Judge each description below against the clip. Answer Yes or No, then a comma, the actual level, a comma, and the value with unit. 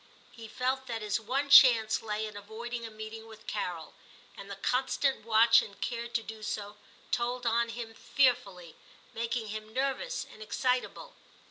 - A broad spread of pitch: No, narrow, 2.4 semitones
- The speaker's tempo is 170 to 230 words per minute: No, average, 160 wpm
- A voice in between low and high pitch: No, high, 225 Hz